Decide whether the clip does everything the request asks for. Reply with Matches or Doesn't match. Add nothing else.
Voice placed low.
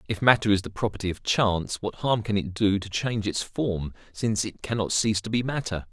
Matches